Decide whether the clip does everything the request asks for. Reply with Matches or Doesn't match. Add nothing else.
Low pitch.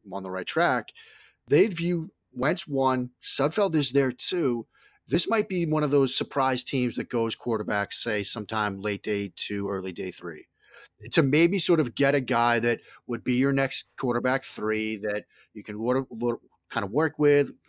Matches